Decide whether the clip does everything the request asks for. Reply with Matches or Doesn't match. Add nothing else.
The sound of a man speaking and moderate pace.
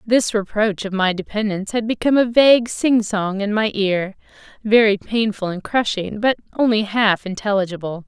Doesn't match